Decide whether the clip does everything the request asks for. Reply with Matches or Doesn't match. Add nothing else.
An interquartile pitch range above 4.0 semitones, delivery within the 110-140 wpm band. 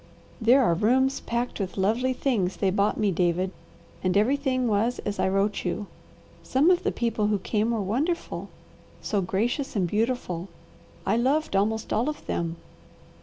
Doesn't match